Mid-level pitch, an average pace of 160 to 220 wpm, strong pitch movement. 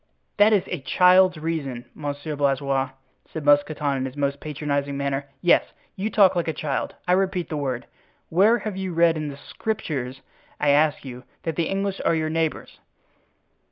No: medium, 155 Hz; average, 175 wpm; average, 4.2 semitones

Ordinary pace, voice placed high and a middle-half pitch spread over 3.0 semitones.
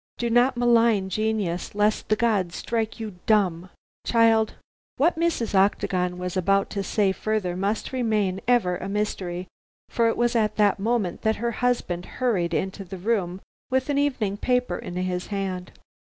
Yes: average, 165 wpm; high, 210 Hz; average, 4.0 semitones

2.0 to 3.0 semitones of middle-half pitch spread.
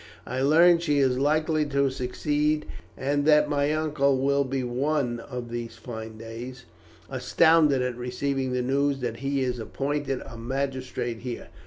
Yes: average, 2.7 semitones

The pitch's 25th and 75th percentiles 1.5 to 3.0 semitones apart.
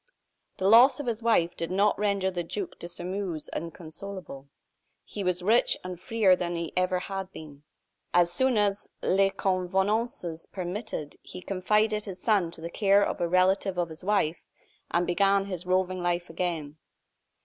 Yes: narrow, 2.6 semitones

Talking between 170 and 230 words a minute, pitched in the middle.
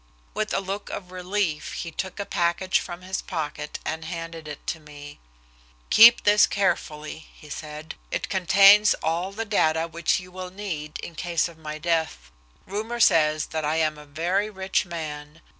Yes: average, 175 wpm; medium, 170 Hz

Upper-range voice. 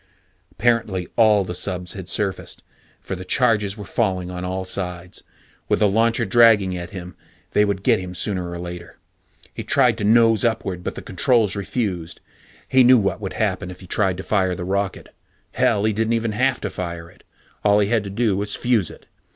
No: low, 100 Hz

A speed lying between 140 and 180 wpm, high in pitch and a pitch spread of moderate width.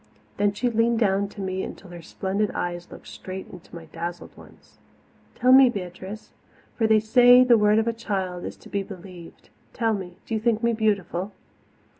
No: average, 195 wpm; high, 205 Hz; average, 3.5 semitones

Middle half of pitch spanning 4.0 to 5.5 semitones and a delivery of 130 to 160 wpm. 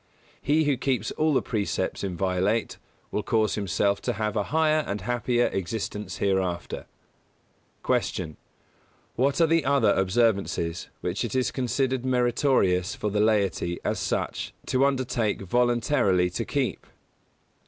Yes: average, 5.0 semitones; slow, 135 wpm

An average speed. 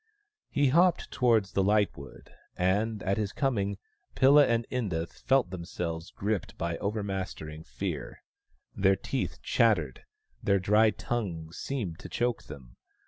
No: slow, 130 wpm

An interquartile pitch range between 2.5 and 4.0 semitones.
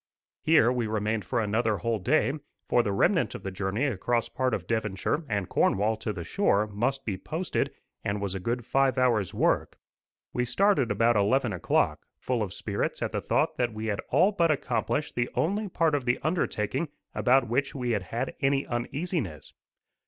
No: average, 4.5 semitones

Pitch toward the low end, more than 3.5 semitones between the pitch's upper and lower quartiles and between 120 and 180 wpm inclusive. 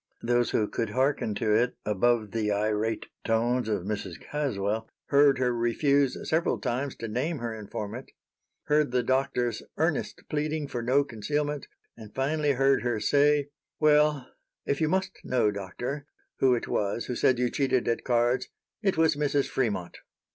Yes: low, 125 Hz; average, 4.2 semitones; average, 160 wpm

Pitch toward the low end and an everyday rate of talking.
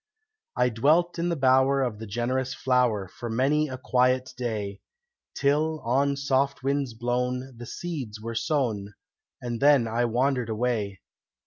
Yes: low, 125 Hz; average, 145 wpm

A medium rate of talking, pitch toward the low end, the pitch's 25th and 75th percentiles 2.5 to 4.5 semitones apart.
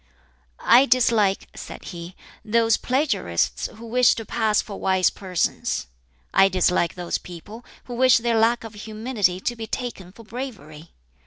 No: average, 150 wpm; high, 220 Hz; average, 4.2 semitones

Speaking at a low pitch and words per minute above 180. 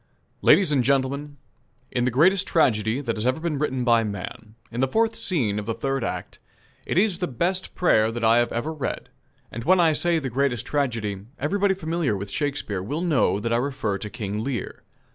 Yes: low, 130 Hz; average, 200 wpm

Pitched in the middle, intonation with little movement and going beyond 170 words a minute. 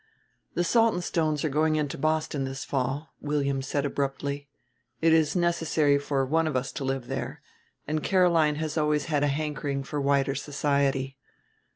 No: medium, 145 Hz; narrow, 2.2 semitones; average, 160 wpm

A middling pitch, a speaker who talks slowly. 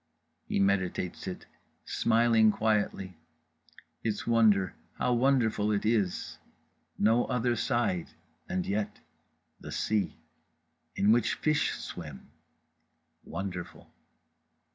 No: low, 105 Hz; slow, 90 wpm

